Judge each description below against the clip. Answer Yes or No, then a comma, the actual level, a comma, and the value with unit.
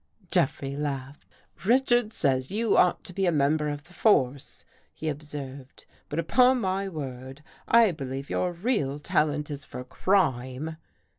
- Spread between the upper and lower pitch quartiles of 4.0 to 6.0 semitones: Yes, wide, 5.6 semitones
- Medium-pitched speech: Yes, medium, 150 Hz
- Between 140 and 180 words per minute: Yes, average, 160 wpm